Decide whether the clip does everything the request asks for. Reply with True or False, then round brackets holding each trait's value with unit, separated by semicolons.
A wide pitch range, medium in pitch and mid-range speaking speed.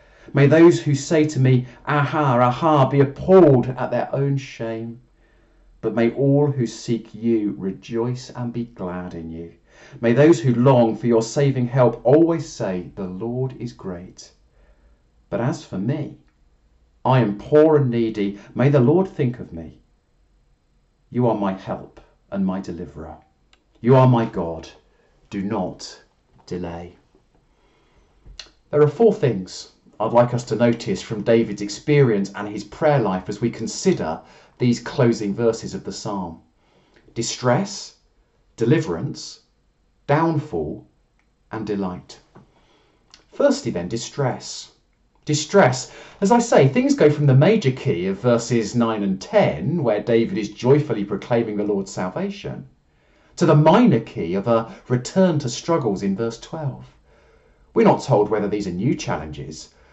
False (5.8 semitones; 120 Hz; 145 wpm)